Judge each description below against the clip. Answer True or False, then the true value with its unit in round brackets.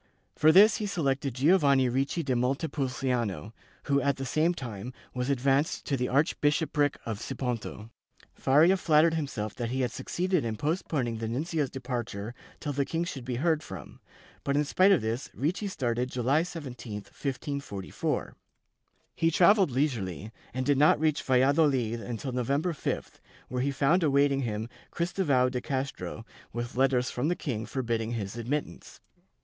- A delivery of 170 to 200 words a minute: False (155 wpm)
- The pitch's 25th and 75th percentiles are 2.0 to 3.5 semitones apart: False (3.9 semitones)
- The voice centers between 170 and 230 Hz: False (135 Hz)